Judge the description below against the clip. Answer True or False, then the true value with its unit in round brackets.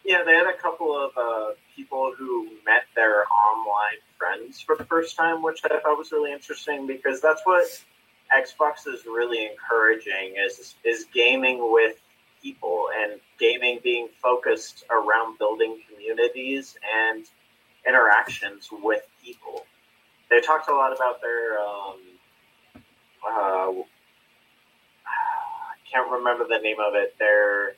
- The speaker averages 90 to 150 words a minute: True (135 wpm)